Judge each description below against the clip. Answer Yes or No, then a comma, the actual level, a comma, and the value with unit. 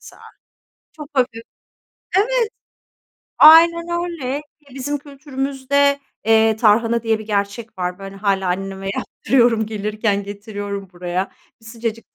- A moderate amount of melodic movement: No, wide, 5.8 semitones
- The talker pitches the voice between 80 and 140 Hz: No, high, 225 Hz